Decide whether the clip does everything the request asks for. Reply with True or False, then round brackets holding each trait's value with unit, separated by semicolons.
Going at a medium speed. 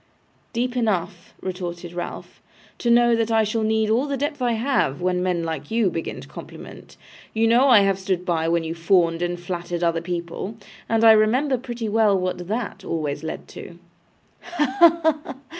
True (185 wpm)